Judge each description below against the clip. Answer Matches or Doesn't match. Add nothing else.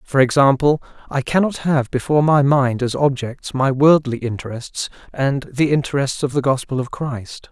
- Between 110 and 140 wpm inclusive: Doesn't match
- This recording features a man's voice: Matches